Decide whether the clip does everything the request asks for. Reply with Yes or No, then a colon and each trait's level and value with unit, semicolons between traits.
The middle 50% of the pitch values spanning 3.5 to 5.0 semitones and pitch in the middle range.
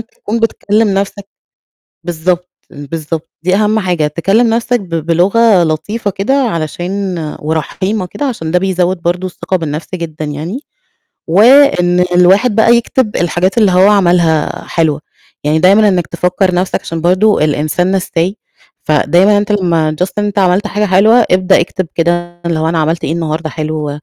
Yes: average, 3.8 semitones; medium, 180 Hz